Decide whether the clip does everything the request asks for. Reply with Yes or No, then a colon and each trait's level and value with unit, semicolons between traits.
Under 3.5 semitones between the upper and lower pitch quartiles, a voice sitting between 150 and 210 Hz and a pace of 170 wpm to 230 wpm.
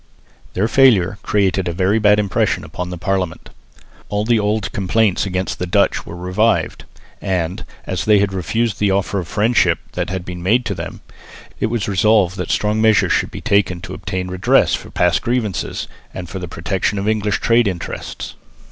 No: average, 2.7 semitones; low, 100 Hz; average, 185 wpm